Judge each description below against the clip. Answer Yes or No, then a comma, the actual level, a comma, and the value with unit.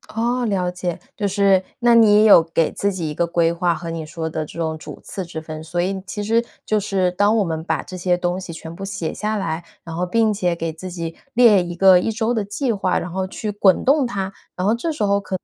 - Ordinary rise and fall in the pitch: Yes, average, 3.6 semitones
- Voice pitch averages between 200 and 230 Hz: No, medium, 185 Hz